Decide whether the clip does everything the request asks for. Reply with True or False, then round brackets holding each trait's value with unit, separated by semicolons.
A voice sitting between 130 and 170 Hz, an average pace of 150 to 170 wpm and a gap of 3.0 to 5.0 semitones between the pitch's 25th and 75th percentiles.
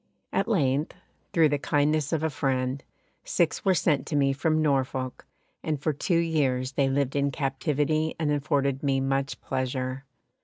False (140 Hz; 160 wpm; 2.5 semitones)